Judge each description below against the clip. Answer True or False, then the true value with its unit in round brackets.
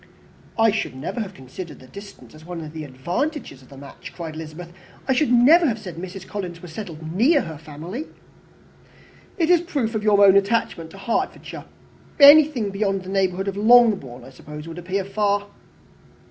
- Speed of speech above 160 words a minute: True (190 wpm)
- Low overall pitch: False (195 Hz)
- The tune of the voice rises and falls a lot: True (5.7 semitones)